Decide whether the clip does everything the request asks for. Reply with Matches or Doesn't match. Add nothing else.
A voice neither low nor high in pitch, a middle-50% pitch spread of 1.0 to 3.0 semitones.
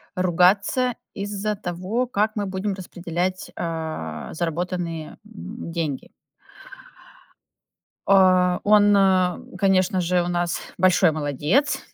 Matches